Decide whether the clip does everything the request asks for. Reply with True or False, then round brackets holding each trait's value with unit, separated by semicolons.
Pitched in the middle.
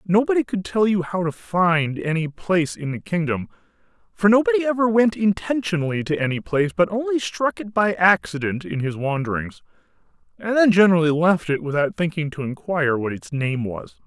True (165 Hz)